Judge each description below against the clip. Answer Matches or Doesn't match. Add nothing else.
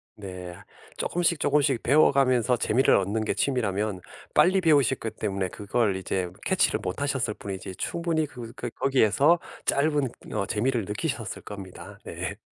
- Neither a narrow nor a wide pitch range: Doesn't match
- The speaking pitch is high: Doesn't match